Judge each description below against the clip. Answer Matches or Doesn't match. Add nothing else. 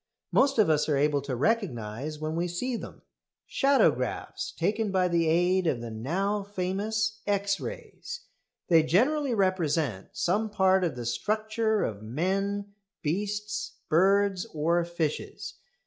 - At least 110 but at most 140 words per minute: Matches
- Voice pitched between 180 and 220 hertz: Matches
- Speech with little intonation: Doesn't match